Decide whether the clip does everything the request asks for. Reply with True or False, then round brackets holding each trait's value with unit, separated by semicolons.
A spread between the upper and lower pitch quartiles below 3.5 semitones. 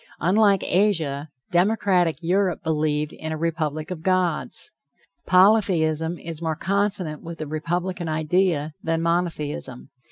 True (2.9 semitones)